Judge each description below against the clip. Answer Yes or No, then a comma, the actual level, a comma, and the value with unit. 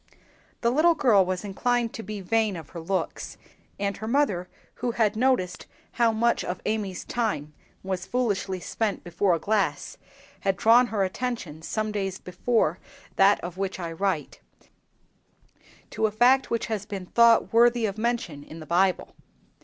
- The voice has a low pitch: No, high, 205 Hz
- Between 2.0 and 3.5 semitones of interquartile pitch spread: No, average, 4.1 semitones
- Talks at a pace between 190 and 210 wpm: No, average, 165 wpm